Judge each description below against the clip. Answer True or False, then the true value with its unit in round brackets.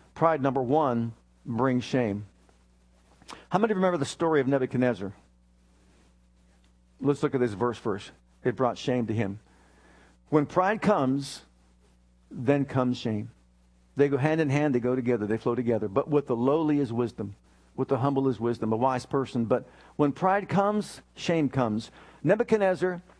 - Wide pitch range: True (6.4 semitones)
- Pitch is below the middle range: True (125 Hz)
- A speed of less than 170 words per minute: True (160 wpm)